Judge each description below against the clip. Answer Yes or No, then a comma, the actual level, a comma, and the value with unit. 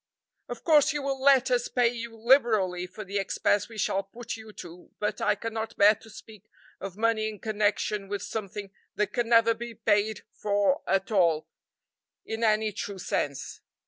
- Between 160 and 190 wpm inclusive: Yes, average, 175 wpm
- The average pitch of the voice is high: Yes, high, 215 Hz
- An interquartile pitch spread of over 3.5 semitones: No, narrow, 2.5 semitones